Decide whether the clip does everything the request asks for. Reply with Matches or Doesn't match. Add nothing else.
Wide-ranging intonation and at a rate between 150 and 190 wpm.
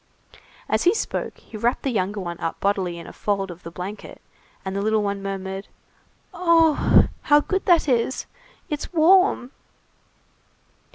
Matches